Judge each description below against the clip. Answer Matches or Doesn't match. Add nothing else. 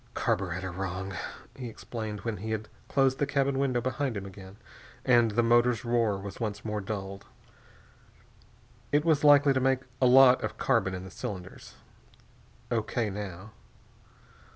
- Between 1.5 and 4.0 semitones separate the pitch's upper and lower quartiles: Doesn't match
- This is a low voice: Matches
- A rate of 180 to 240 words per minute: Doesn't match